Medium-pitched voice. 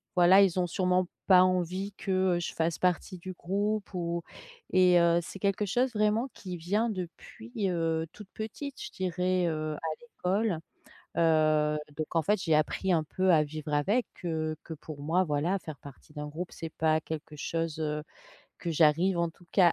Yes: medium, 175 Hz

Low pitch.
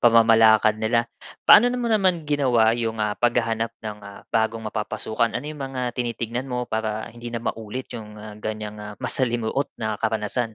Yes: low, 115 Hz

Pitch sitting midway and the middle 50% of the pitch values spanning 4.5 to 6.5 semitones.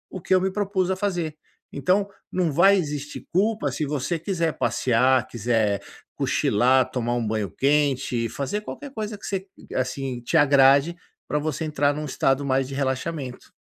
Yes: medium, 145 Hz; wide, 5.6 semitones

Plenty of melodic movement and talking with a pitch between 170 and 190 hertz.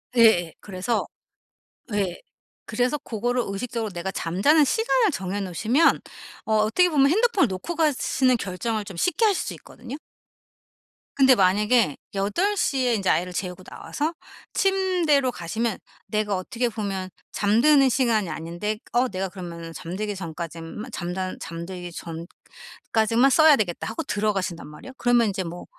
No: wide, 5.8 semitones; high, 215 Hz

